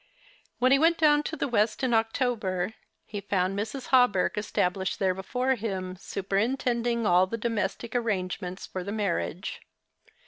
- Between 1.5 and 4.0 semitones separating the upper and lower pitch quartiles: No, average, 4.5 semitones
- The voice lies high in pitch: Yes, high, 215 Hz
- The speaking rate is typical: Yes, average, 150 wpm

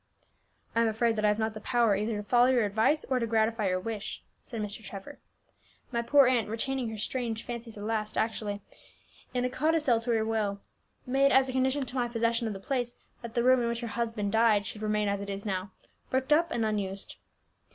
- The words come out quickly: Yes, fast, 225 wpm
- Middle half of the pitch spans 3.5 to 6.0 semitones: No, average, 2.7 semitones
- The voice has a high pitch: Yes, high, 230 Hz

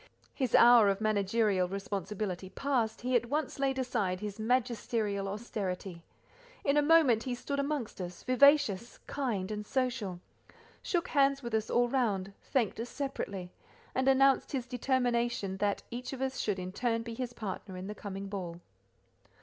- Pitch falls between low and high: No, high, 230 Hz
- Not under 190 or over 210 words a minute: No, average, 160 wpm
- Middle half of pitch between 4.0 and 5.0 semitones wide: Yes, average, 4.6 semitones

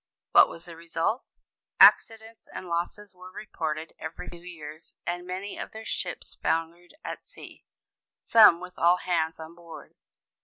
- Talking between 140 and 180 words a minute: Yes, average, 150 wpm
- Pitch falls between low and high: Yes, medium, 175 Hz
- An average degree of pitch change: No, narrow, 2.1 semitones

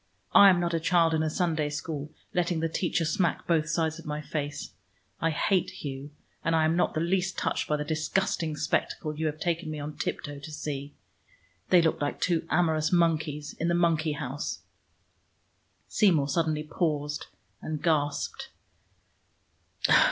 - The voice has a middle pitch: Yes, medium, 160 Hz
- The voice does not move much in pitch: Yes, narrow, 2.1 semitones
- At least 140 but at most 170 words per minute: Yes, average, 165 wpm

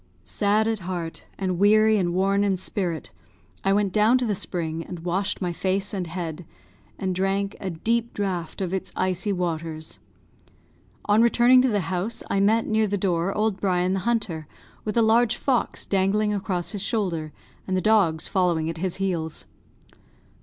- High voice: Yes, high, 195 Hz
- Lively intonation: No, average, 3.2 semitones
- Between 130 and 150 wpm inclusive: No, average, 175 wpm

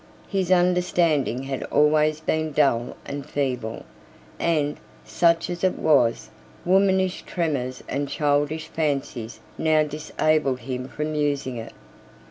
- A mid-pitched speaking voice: Yes, medium, 150 Hz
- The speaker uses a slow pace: Yes, slow, 115 wpm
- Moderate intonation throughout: Yes, average, 3.3 semitones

